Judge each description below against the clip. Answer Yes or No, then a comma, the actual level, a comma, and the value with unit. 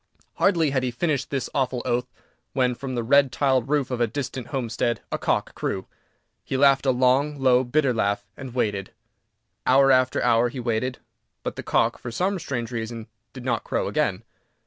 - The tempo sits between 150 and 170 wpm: No, average, 185 wpm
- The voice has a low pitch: Yes, low, 130 Hz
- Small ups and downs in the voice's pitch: Yes, narrow, 2.3 semitones